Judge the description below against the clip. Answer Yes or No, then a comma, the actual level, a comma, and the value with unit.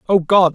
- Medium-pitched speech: Yes, medium, 180 Hz